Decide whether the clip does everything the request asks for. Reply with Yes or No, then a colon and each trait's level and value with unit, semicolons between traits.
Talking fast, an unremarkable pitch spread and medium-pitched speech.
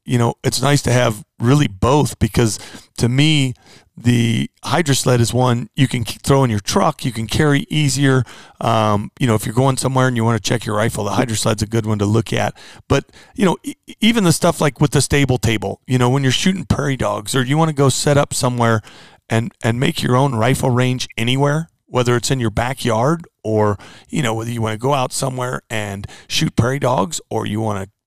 No: fast, 230 wpm; average, 3.9 semitones; low, 125 Hz